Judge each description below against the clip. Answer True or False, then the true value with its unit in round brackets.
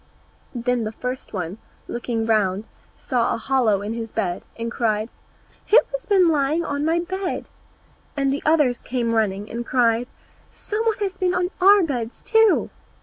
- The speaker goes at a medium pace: True (165 wpm)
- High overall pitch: True (250 Hz)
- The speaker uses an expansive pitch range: True (7.2 semitones)